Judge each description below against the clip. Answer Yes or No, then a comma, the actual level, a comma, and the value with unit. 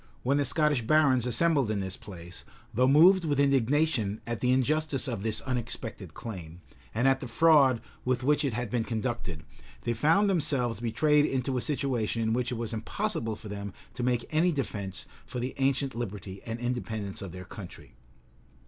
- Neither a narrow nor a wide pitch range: Yes, average, 4.3 semitones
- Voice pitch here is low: Yes, low, 125 Hz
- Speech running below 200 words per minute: Yes, average, 180 wpm